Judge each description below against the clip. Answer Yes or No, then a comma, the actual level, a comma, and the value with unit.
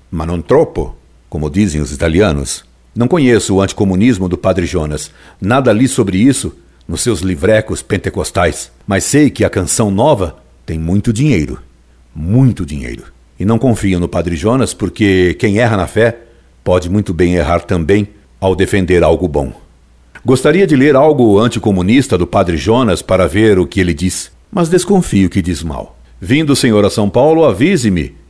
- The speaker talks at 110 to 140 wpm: No, average, 165 wpm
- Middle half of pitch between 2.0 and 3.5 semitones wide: No, average, 4.9 semitones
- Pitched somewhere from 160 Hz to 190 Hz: No, very low, 95 Hz